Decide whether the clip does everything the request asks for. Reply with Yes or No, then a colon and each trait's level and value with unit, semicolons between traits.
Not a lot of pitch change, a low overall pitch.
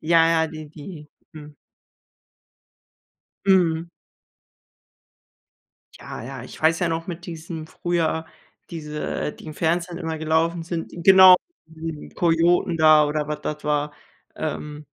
No: narrow, 1.9 semitones; medium, 160 Hz